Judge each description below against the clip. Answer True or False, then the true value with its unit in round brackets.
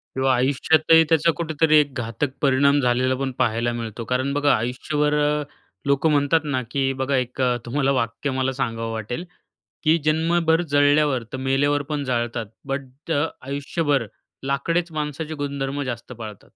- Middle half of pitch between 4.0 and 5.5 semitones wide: False (2.7 semitones)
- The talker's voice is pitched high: False (140 Hz)